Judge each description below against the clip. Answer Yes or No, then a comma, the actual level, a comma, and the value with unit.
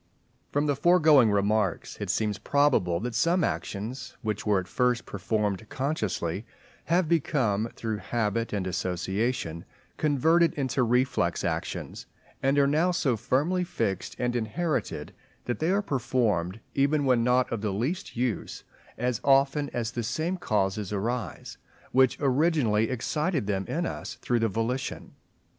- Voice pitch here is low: Yes, low, 125 Hz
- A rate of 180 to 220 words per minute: No, average, 145 wpm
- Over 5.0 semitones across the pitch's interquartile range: Yes, wide, 5.4 semitones